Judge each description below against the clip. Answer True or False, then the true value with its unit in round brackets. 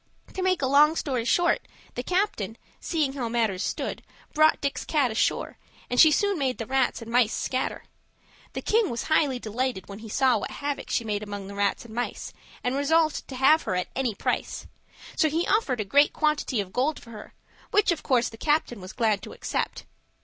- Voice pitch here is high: True (260 Hz)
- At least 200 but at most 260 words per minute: True (205 wpm)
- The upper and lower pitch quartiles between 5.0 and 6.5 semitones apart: True (5.4 semitones)